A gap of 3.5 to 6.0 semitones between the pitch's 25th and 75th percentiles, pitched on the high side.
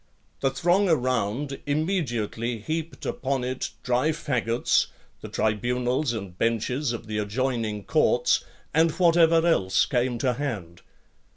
No: average, 5.0 semitones; low, 125 Hz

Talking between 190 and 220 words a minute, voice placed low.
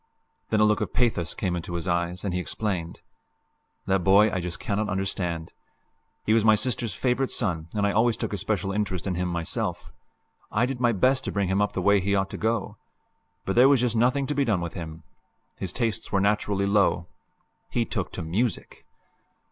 Yes: fast, 205 wpm; low, 100 Hz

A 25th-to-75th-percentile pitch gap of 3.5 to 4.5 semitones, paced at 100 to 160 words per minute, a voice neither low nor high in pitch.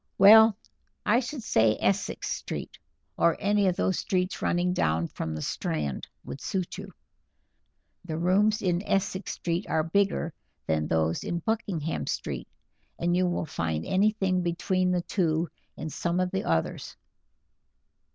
Yes: average, 3.8 semitones; average, 145 wpm; medium, 180 Hz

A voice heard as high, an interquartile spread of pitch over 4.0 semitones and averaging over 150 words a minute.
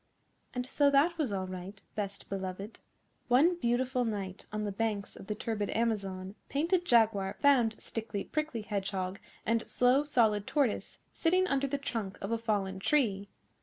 Yes: high, 225 Hz; average, 5.1 semitones; average, 160 wpm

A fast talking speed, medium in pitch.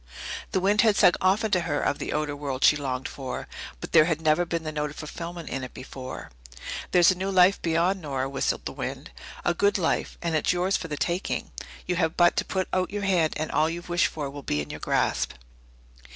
Yes: fast, 230 wpm; medium, 165 Hz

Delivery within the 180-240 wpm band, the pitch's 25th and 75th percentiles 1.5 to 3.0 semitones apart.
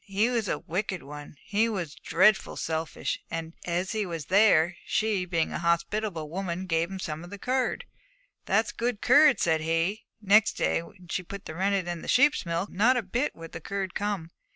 No: average, 200 wpm; average, 4.2 semitones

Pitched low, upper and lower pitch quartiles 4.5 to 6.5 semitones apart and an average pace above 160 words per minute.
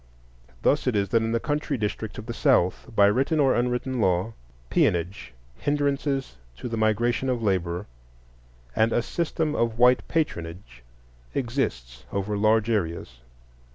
No: low, 115 Hz; average, 5.0 semitones; average, 145 wpm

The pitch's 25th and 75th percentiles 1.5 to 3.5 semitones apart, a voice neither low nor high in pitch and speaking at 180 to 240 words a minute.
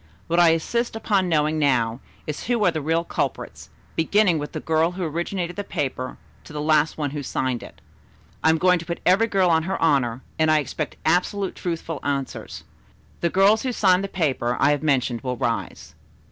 No: average, 3.9 semitones; medium, 160 Hz; average, 200 wpm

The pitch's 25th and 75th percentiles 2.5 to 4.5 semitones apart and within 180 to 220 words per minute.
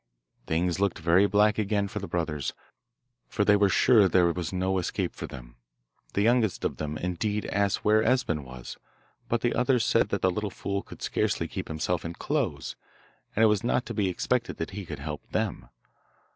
Yes: average, 3.9 semitones; average, 195 wpm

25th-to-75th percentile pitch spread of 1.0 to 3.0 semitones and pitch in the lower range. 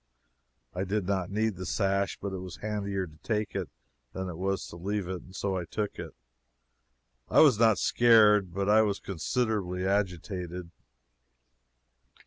Yes: narrow, 2.4 semitones; low, 100 Hz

